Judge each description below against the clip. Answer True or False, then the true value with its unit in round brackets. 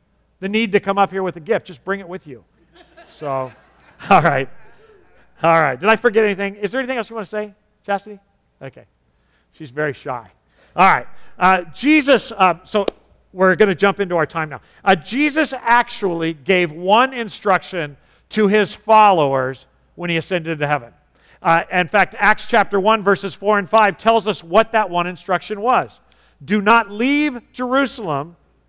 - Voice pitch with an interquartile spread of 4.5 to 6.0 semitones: True (4.8 semitones)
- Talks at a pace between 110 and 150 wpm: False (180 wpm)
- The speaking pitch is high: True (195 Hz)